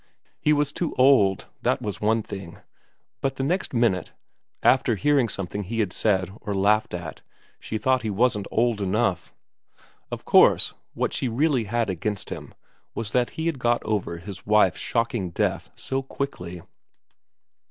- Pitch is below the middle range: Yes, low, 110 Hz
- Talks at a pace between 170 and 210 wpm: No, average, 160 wpm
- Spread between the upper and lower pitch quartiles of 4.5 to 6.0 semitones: Yes, average, 4.8 semitones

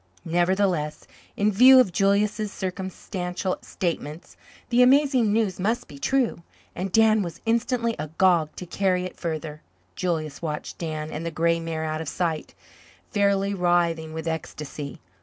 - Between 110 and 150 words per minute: Yes, average, 140 wpm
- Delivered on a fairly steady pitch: No, average, 4.2 semitones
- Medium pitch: Yes, medium, 180 Hz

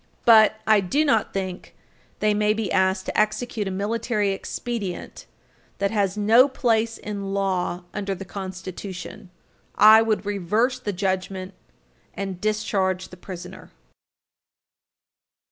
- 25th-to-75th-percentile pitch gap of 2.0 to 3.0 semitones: Yes, narrow, 2.4 semitones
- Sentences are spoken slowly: Yes, slow, 125 wpm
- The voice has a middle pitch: No, high, 200 Hz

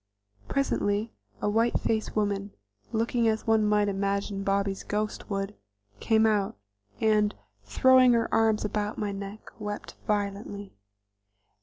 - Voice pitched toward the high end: Yes, high, 210 Hz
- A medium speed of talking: No, slow, 125 wpm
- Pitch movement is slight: Yes, narrow, 1.6 semitones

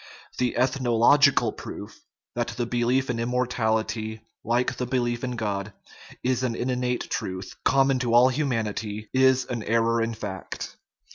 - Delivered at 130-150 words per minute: Yes, average, 140 wpm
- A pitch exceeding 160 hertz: No, low, 120 Hz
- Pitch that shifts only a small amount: Yes, narrow, 2.2 semitones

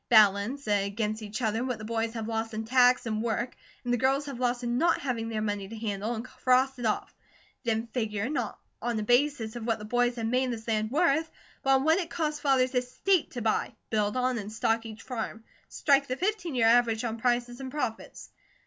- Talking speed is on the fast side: Yes, fast, 220 wpm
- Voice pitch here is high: Yes, high, 240 Hz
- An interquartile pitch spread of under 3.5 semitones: Yes, average, 2.7 semitones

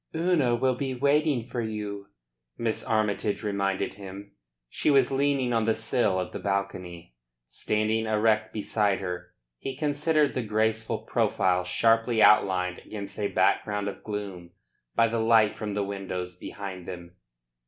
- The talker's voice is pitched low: Yes, low, 105 Hz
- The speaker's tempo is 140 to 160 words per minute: Yes, average, 145 wpm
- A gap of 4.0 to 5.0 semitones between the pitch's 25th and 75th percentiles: No, average, 3.2 semitones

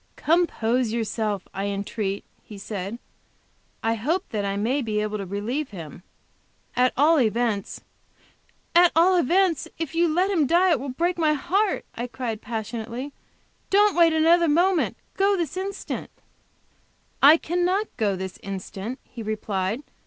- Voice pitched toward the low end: No, very high, 255 Hz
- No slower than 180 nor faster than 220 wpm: No, average, 150 wpm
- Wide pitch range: Yes, wide, 8.1 semitones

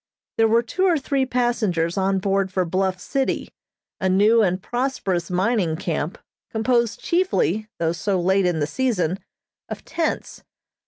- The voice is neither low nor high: No, high, 195 Hz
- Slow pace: No, average, 150 wpm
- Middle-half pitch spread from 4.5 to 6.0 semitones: Yes, average, 5.0 semitones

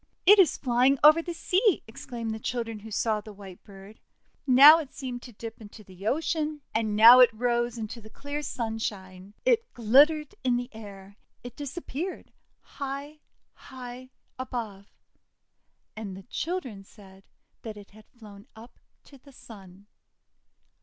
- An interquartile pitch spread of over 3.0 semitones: Yes, average, 4.7 semitones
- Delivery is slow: No, average, 150 wpm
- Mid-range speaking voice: No, high, 235 Hz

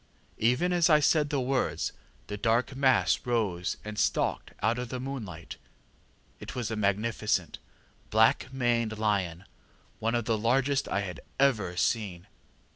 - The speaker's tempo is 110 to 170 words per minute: Yes, average, 145 wpm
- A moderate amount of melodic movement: Yes, average, 4.0 semitones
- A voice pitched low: Yes, low, 115 Hz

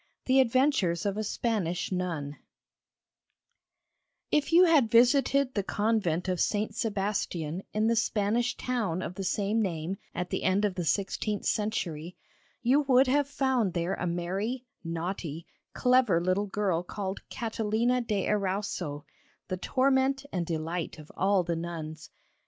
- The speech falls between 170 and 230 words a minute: No, average, 140 wpm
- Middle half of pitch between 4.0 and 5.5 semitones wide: Yes, average, 5.2 semitones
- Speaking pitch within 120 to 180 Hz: No, high, 200 Hz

